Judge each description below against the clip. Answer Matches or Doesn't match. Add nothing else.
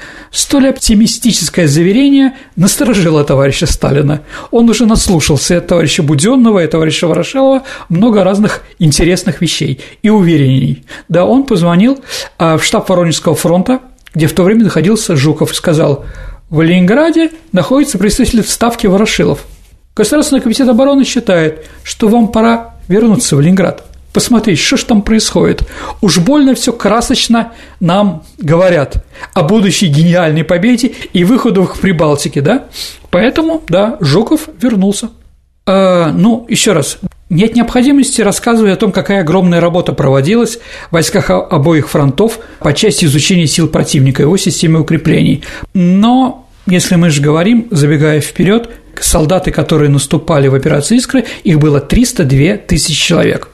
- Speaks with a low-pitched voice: Doesn't match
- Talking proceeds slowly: Doesn't match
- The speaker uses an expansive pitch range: Matches